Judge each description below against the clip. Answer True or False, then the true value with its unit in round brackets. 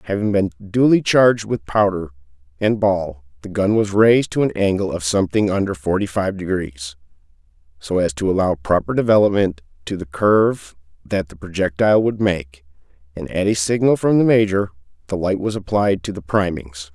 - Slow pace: False (175 wpm)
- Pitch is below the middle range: True (95 Hz)